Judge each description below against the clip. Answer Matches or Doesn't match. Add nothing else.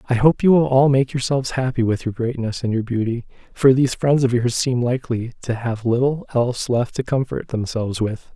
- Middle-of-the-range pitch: Doesn't match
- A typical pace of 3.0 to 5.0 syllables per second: Doesn't match